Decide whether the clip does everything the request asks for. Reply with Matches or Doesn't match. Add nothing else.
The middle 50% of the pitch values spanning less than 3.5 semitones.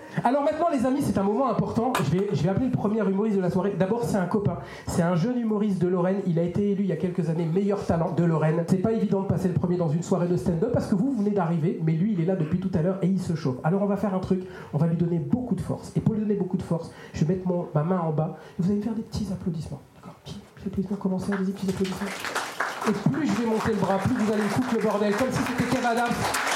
Matches